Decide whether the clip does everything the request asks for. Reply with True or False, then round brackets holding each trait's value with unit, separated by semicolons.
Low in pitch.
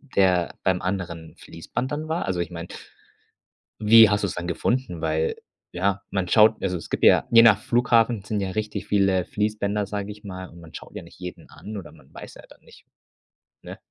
True (100 Hz)